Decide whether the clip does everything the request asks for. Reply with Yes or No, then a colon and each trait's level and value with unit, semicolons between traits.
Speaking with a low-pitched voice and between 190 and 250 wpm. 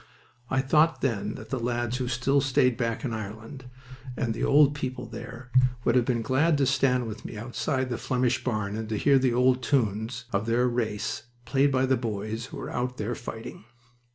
Yes: low, 125 Hz; average, 200 wpm